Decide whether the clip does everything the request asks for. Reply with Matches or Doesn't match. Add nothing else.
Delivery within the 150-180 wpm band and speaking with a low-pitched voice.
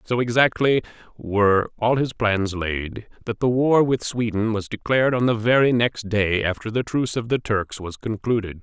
Doesn't match